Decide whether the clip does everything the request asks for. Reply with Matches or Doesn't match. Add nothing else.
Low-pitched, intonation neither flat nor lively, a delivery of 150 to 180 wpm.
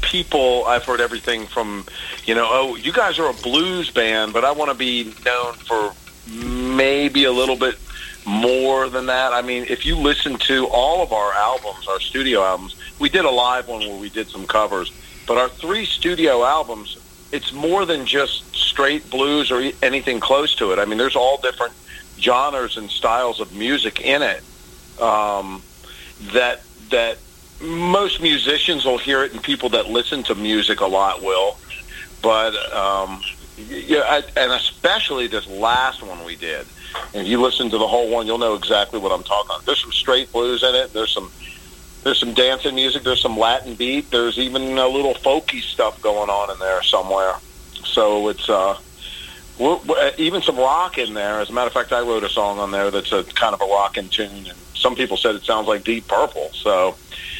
Doesn't match